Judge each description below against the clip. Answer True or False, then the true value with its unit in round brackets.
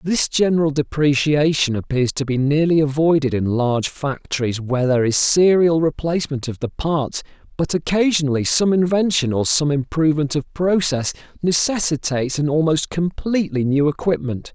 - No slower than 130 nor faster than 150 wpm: True (140 wpm)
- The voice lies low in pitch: False (150 Hz)